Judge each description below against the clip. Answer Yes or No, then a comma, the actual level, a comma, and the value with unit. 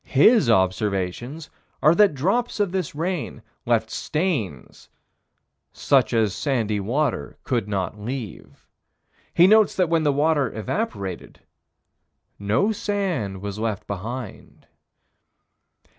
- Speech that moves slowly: Yes, slow, 110 wpm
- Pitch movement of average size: No, wide, 8.8 semitones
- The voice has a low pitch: Yes, low, 130 Hz